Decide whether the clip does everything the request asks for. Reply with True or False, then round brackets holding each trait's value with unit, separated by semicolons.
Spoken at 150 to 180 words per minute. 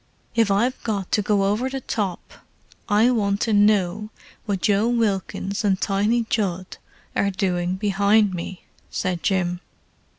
False (140 wpm)